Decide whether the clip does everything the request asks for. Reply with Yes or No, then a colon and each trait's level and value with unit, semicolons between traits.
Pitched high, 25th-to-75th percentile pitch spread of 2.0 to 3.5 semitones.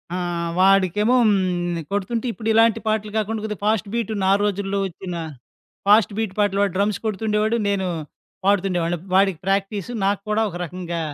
Yes: high, 200 Hz; narrow, 2.5 semitones